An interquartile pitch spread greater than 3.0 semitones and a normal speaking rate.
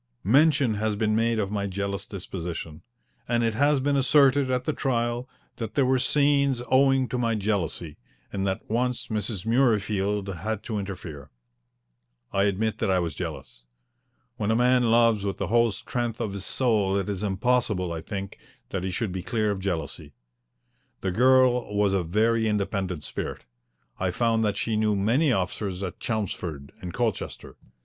Yes: average, 3.8 semitones; average, 170 wpm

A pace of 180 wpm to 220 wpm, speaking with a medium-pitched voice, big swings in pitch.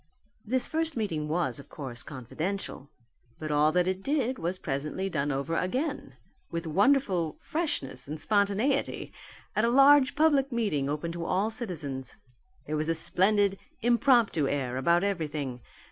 No: average, 145 wpm; medium, 180 Hz; wide, 7.7 semitones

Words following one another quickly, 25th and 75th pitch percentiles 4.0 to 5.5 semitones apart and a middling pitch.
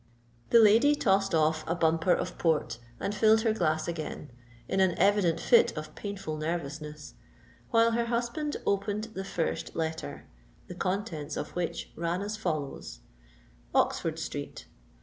No: average, 145 wpm; average, 5.1 semitones; medium, 180 Hz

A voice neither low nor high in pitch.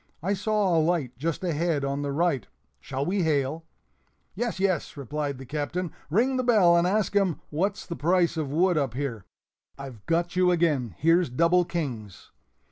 Yes: medium, 165 Hz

